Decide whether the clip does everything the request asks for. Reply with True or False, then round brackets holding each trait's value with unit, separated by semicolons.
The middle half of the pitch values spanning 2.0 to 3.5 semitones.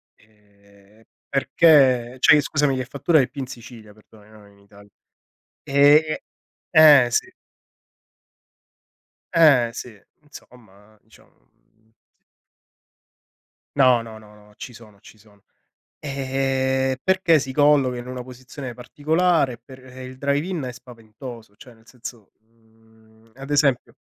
False (4.0 semitones)